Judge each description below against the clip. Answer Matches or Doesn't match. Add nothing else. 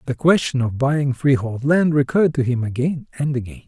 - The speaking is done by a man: Matches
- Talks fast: Doesn't match